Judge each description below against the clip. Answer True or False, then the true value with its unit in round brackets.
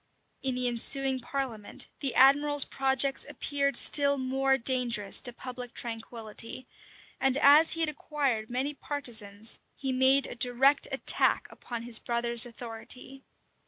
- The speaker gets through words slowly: True (130 wpm)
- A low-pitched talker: False (260 Hz)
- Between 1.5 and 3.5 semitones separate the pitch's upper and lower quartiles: True (2.6 semitones)